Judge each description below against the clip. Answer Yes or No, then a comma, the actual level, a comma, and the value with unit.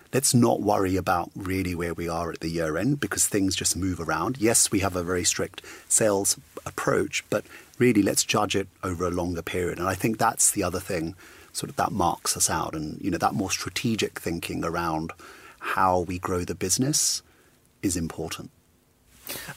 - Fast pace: No, average, 190 wpm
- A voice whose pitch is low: Yes, very low, 90 Hz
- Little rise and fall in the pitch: Yes, narrow, 2.3 semitones